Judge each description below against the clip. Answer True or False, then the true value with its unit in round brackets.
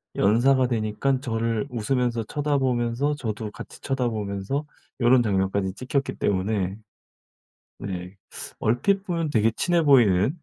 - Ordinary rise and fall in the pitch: True (4.6 semitones)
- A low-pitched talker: True (120 Hz)